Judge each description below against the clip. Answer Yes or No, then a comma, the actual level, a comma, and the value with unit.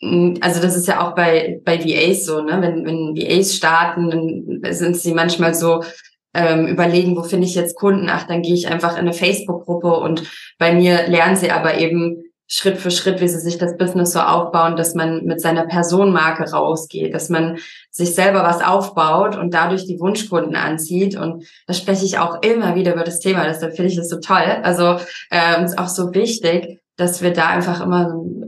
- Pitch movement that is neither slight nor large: No, narrow, 1.4 semitones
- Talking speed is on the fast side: Yes, fast, 205 wpm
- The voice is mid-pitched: Yes, medium, 175 Hz